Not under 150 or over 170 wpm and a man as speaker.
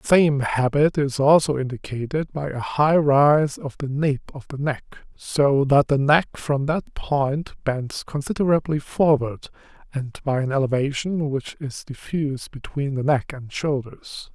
Yes: average, 160 wpm; male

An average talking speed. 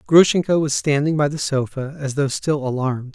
Yes: average, 190 wpm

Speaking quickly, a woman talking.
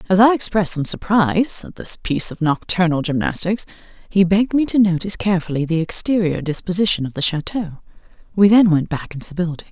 No: average, 185 wpm; female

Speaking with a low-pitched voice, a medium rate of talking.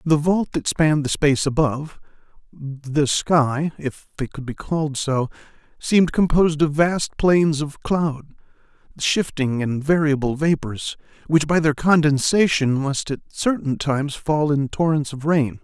No: medium, 150 Hz; average, 150 wpm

